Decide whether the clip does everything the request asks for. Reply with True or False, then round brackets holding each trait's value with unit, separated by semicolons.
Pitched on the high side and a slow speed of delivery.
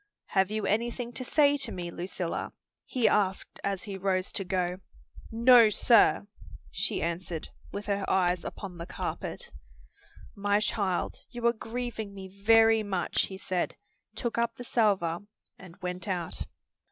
False (200 Hz; 150 wpm)